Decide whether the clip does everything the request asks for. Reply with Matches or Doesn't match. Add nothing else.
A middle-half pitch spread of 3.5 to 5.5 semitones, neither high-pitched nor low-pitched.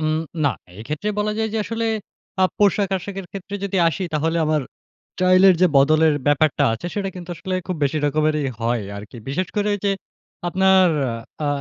Matches